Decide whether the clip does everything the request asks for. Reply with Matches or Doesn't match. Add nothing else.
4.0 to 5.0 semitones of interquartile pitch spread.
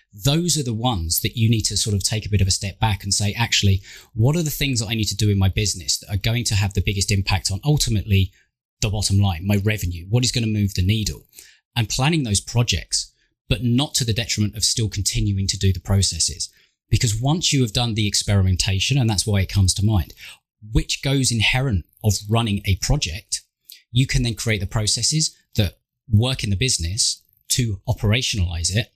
Doesn't match